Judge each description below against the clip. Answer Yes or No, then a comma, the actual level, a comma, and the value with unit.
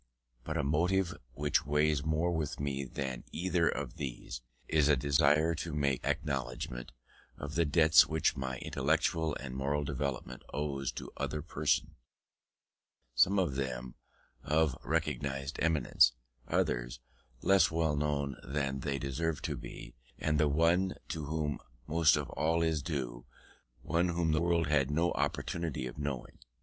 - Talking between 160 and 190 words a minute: No, average, 145 wpm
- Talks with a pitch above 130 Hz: No, very low, 75 Hz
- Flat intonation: No, average, 3.1 semitones